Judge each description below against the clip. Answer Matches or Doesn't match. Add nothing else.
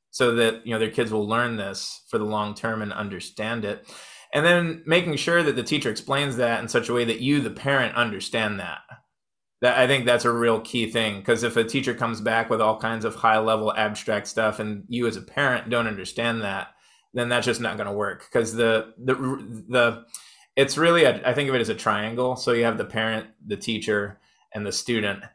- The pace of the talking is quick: Matches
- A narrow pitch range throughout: Matches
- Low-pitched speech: Matches